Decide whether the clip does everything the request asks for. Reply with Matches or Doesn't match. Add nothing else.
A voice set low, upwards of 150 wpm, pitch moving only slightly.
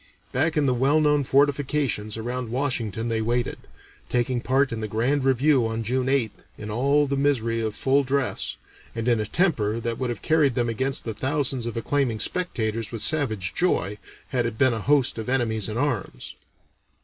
Doesn't match